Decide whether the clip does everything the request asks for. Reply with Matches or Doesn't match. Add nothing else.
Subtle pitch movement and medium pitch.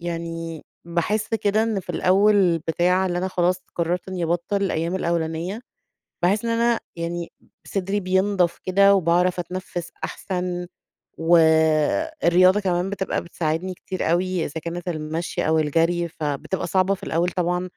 Matches